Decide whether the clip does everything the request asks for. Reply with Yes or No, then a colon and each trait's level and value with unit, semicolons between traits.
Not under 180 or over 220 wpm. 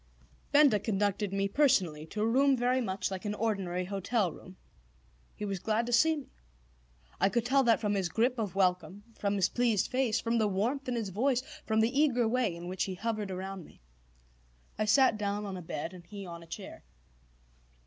Yes: average, 200 wpm